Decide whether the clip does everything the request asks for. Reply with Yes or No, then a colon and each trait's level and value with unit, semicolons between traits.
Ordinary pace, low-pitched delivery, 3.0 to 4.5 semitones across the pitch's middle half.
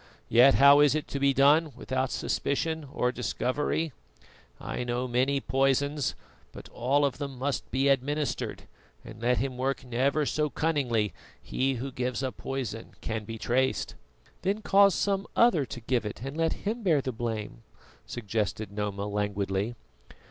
Yes: average, 155 wpm; low, 130 Hz; average, 3.4 semitones